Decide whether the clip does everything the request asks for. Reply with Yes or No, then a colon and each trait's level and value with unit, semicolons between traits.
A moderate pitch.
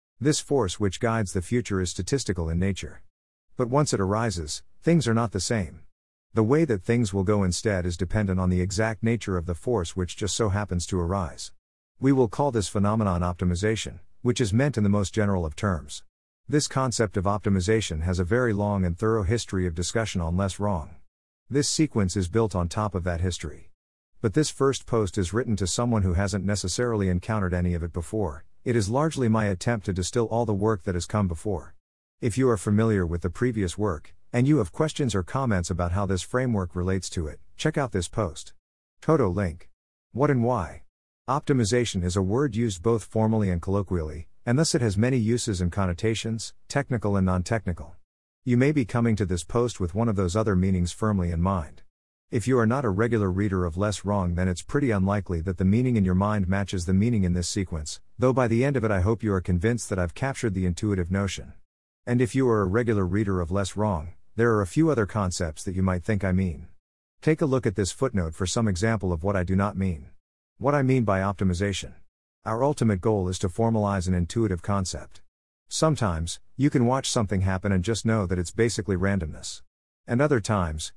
No: low, 100 Hz